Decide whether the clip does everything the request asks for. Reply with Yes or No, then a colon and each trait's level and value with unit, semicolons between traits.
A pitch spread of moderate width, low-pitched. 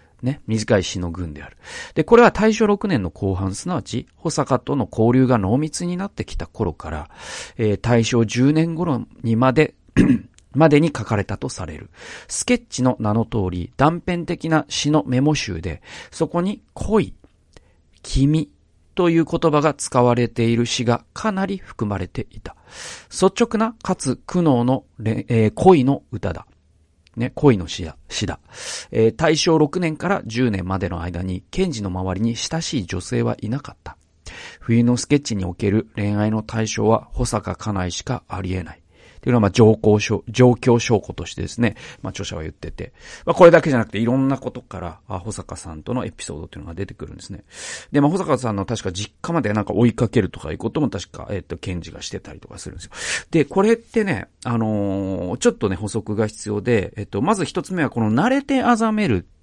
No: wide, 7.3 semitones; low, 115 Hz